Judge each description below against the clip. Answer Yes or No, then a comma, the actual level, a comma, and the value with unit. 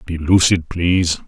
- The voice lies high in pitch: No, very low, 85 Hz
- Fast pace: No, average, 140 wpm